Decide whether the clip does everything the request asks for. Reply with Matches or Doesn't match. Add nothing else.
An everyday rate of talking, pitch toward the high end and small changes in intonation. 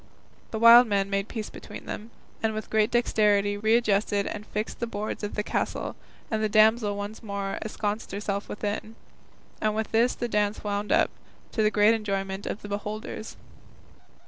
Matches